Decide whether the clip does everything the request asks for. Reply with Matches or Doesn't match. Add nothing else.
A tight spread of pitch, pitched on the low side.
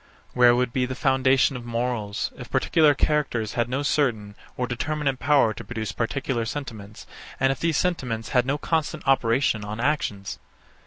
Doesn't match